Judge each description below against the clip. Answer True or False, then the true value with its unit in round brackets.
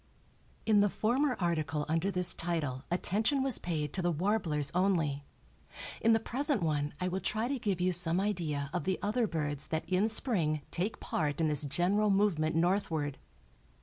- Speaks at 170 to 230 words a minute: True (175 wpm)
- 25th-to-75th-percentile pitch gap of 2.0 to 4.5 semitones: False (5.1 semitones)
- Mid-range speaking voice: True (175 Hz)